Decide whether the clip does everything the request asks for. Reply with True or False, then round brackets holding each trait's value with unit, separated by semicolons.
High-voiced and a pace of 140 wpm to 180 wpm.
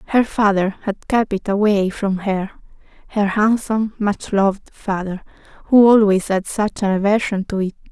True (205 Hz; 150 wpm)